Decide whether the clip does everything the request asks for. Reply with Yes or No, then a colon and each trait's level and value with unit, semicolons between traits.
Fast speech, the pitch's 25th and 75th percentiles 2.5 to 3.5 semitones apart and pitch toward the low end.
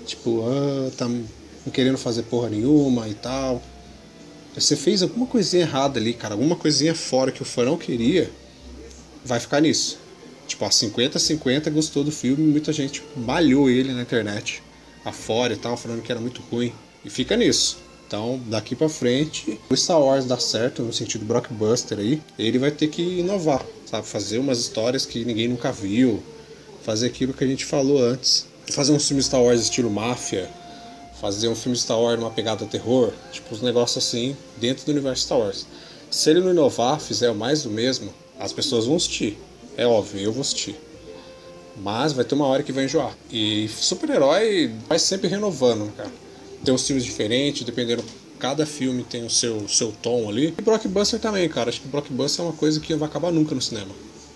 No: fast, 190 wpm; average, 4.1 semitones; low, 130 Hz